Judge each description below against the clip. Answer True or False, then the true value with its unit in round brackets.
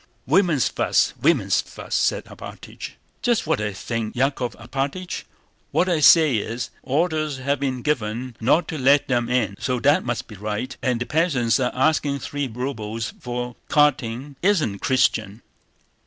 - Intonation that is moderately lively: True (4.1 semitones)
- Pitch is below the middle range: True (130 Hz)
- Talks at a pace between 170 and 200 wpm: False (155 wpm)